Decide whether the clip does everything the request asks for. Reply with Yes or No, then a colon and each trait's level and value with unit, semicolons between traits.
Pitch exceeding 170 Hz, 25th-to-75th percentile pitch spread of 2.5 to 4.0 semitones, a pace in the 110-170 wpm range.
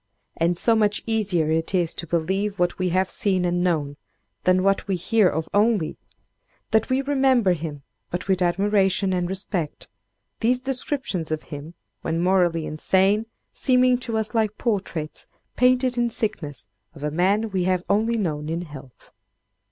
No: high, 190 Hz; average, 4.6 semitones; average, 160 wpm